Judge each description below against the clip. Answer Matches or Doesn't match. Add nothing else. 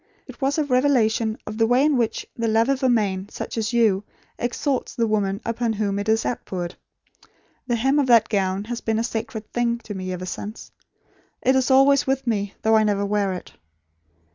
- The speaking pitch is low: Doesn't match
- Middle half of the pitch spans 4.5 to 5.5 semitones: Doesn't match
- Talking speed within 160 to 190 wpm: Doesn't match